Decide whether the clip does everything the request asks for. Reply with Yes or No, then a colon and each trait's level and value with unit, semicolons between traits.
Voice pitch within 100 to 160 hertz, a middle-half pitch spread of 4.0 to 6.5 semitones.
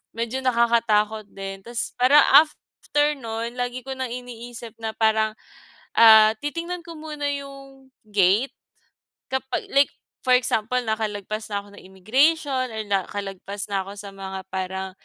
No: high, 230 Hz; average, 4.4 semitones